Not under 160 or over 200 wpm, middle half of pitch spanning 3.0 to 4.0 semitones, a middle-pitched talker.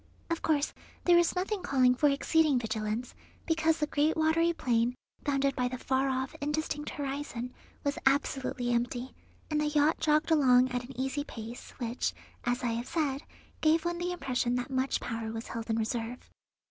No: average, 175 wpm; average, 3.7 semitones; very high, 270 Hz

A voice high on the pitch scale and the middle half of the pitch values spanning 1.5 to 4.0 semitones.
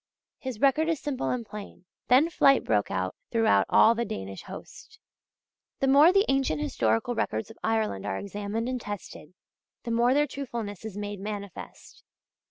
No: high, 225 Hz; average, 4.8 semitones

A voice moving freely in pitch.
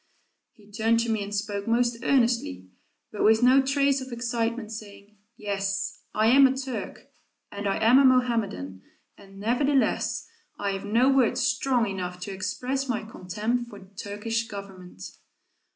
No: average, 3.7 semitones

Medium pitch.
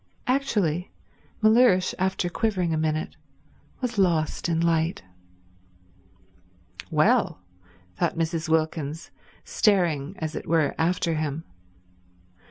Yes: medium, 165 Hz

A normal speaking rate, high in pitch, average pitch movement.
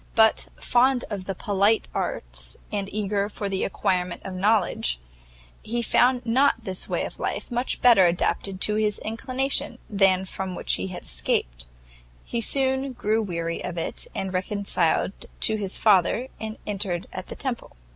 Yes: average, 165 wpm; high, 200 Hz; average, 3.6 semitones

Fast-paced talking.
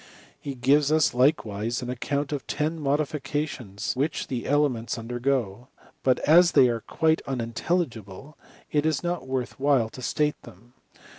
No: average, 150 wpm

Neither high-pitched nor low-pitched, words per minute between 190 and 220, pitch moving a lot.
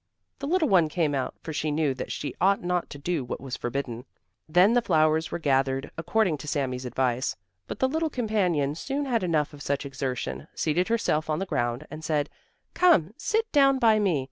Yes: medium, 155 Hz; average, 200 wpm; wide, 7.2 semitones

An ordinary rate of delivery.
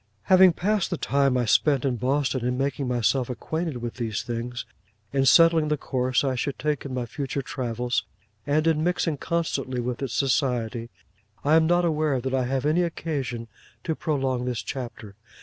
Yes: average, 180 wpm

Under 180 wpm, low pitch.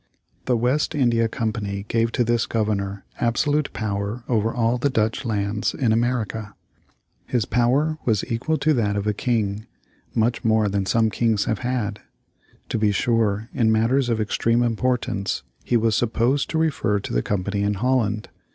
Yes: average, 165 wpm; low, 115 Hz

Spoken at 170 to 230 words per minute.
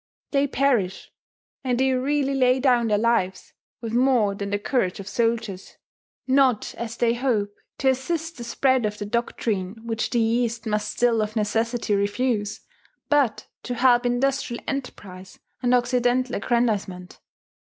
No: average, 145 wpm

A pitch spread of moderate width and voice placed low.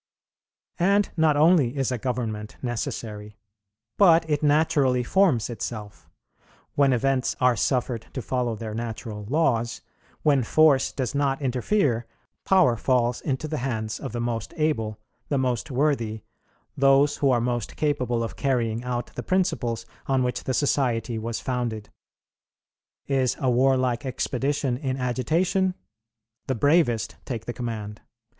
Yes: average, 3.5 semitones; low, 125 Hz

